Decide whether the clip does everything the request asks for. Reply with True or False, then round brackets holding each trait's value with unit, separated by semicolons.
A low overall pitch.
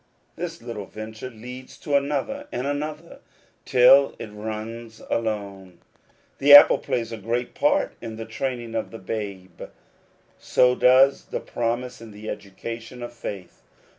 True (115 Hz)